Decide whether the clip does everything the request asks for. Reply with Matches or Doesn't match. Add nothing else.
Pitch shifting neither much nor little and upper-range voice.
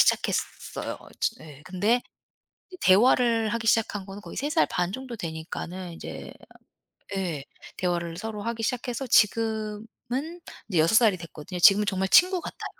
Matches